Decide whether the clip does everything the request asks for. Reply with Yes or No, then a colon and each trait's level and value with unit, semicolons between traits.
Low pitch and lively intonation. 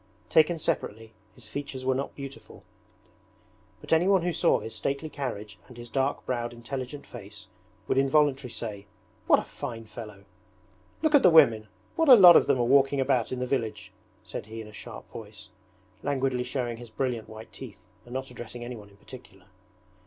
No: low, 125 Hz; average, 3.7 semitones